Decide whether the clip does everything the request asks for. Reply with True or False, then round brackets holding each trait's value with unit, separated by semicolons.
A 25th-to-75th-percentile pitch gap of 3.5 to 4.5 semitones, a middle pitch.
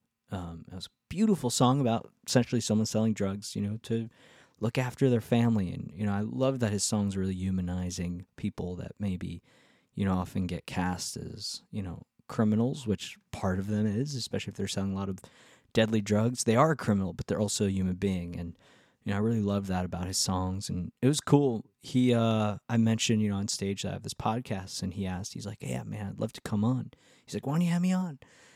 False (4.0 semitones; 105 Hz)